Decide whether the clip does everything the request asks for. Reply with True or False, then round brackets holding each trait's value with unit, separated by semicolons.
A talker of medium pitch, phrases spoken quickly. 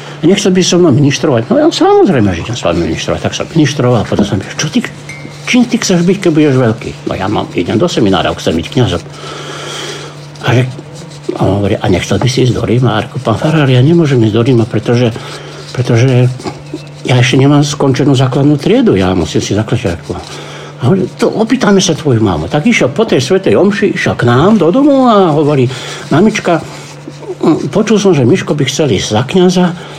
True (145 Hz; 205 wpm)